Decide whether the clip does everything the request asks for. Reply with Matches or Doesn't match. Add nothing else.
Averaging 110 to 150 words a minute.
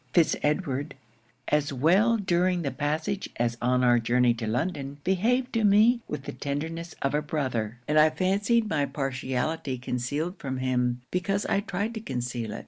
Doesn't match